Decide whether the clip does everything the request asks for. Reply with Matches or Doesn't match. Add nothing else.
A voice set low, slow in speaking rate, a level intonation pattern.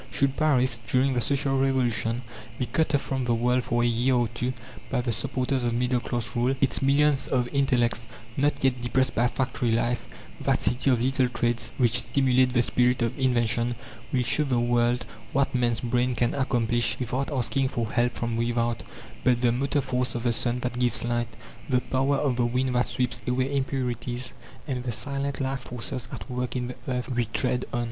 Doesn't match